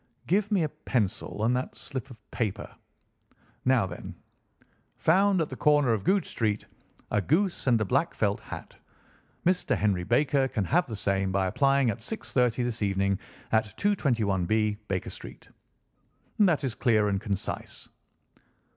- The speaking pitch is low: Yes, low, 120 Hz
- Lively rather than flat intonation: Yes, wide, 6.1 semitones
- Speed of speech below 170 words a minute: Yes, average, 150 wpm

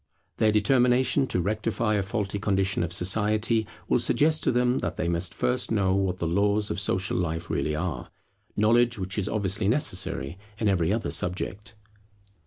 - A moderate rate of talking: Yes, average, 170 wpm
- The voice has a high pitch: No, low, 100 Hz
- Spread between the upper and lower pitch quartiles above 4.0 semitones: No, average, 3.3 semitones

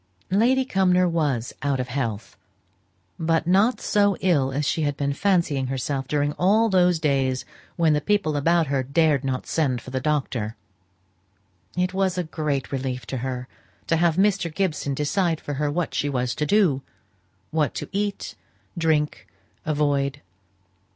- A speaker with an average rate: Yes, average, 160 wpm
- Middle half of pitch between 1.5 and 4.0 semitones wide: No, average, 4.7 semitones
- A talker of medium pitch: Yes, medium, 150 Hz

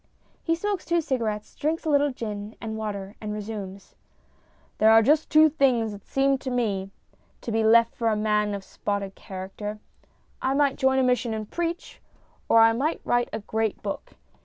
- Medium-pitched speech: No, high, 225 Hz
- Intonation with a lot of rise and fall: No, average, 4.4 semitones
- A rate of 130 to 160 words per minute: No, average, 185 wpm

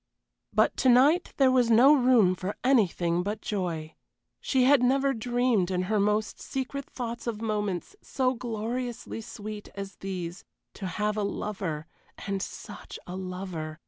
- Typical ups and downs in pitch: Yes, average, 5.0 semitones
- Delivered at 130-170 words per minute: Yes, average, 150 wpm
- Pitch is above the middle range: Yes, high, 215 Hz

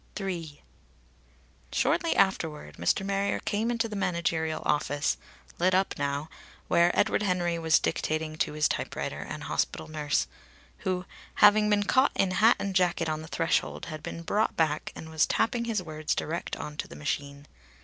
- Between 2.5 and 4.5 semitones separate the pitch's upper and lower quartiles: Yes, average, 4.2 semitones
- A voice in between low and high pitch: Yes, medium, 170 Hz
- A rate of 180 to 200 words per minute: No, average, 165 wpm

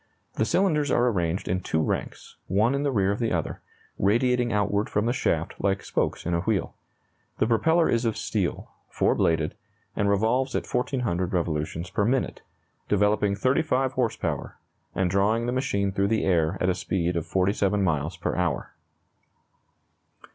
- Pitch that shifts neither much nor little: Yes, average, 5.0 semitones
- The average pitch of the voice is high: No, low, 100 Hz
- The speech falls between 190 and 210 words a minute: No, average, 170 wpm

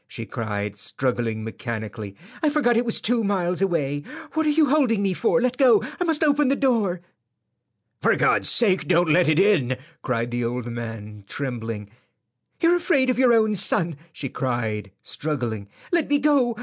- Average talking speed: Yes, average, 175 wpm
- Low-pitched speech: No, medium, 175 Hz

